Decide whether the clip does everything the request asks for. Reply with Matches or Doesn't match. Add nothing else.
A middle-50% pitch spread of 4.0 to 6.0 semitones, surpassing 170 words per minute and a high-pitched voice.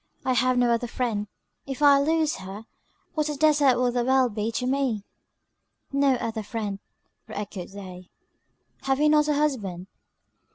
Doesn't match